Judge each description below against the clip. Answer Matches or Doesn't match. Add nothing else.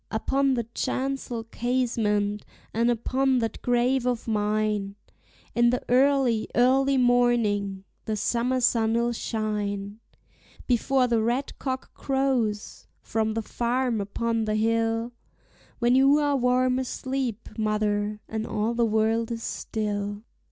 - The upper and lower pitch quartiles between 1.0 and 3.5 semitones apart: Matches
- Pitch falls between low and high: Doesn't match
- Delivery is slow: Matches